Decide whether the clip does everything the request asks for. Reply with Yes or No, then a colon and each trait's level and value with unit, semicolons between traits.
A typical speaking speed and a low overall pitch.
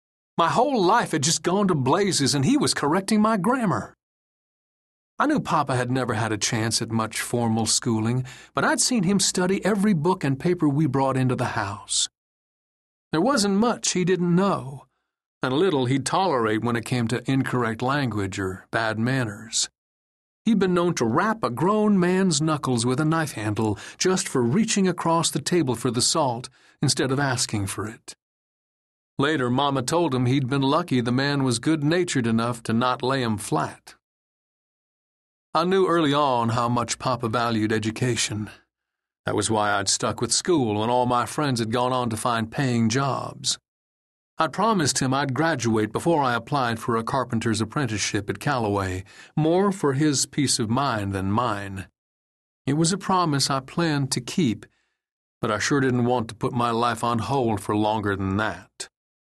Yes: average, 180 wpm; low, 125 Hz